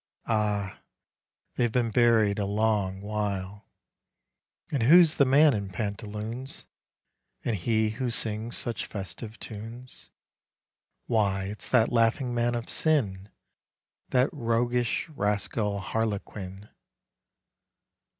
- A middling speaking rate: No, slow, 105 wpm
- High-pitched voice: No, low, 110 Hz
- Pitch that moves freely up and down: No, average, 2.8 semitones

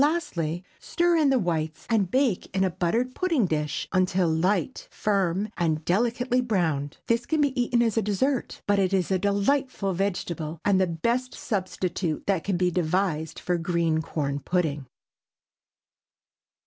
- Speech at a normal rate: Yes, average, 155 wpm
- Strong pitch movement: Yes, wide, 5.8 semitones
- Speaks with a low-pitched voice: No, high, 190 Hz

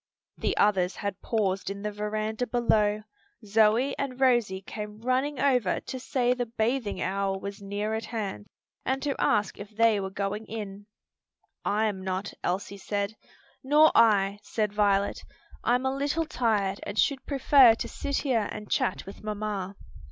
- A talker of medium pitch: No, high, 215 Hz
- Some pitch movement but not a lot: Yes, average, 3.5 semitones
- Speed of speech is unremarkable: Yes, average, 160 wpm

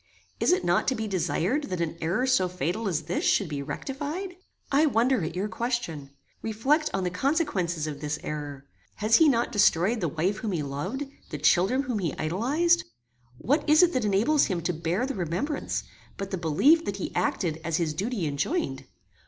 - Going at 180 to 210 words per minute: Yes, average, 195 wpm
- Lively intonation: Yes, wide, 7.9 semitones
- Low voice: No, high, 195 Hz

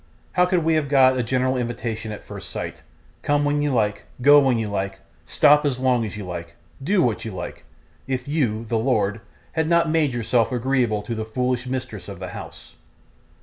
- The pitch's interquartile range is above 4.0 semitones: Yes, average, 4.7 semitones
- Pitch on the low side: Yes, low, 125 Hz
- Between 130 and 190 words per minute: No, average, 200 wpm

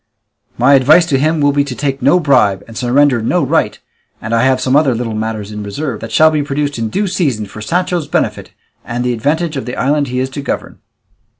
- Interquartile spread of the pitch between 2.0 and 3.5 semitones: No, average, 4.2 semitones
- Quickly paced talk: Yes, fast, 225 wpm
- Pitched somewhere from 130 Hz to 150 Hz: Yes, low, 135 Hz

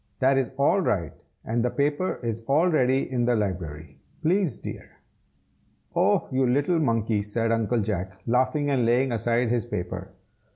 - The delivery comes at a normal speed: Yes, average, 160 wpm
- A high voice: No, low, 120 Hz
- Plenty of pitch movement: No, average, 4.3 semitones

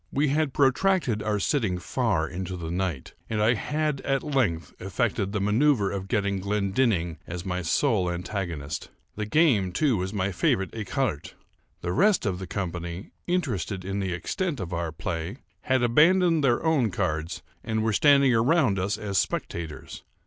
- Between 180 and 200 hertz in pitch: No, low, 100 Hz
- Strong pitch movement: Yes, wide, 6.6 semitones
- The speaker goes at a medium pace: Yes, average, 165 wpm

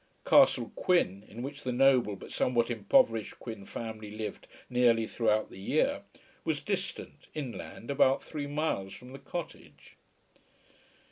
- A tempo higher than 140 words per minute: No, slow, 135 wpm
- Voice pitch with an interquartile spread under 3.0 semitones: No, average, 4.0 semitones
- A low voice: Yes, low, 120 Hz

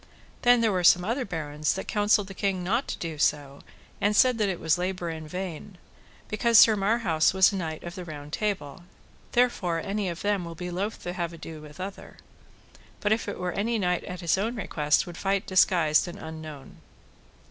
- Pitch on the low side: No, medium, 180 Hz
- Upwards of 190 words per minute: Yes, average, 200 wpm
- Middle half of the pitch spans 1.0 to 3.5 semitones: No, average, 4.1 semitones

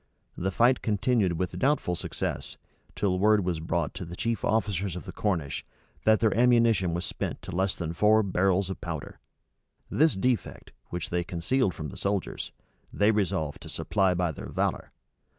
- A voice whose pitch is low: Yes, very low, 95 Hz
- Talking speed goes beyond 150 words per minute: Yes, average, 170 wpm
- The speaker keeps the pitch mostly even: No, average, 3.8 semitones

